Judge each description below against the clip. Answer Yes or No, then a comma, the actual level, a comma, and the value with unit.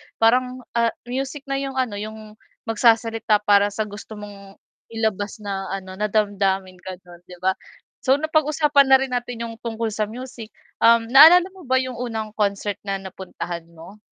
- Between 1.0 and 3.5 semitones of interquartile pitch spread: No, average, 4.0 semitones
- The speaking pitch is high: Yes, high, 220 Hz